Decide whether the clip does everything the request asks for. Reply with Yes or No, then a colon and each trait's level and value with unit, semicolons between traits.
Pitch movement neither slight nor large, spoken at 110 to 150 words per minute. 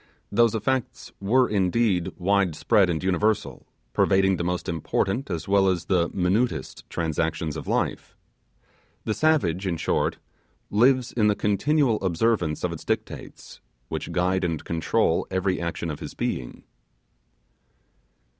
Yes: average, 4.1 semitones; slow, 135 wpm